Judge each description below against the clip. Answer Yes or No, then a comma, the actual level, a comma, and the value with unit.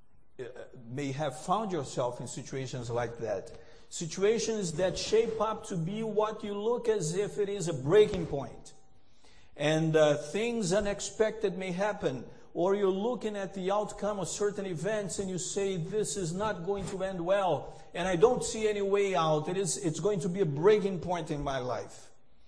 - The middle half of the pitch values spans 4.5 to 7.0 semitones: Yes, average, 5.1 semitones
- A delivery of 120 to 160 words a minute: No, average, 185 wpm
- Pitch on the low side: No, high, 190 Hz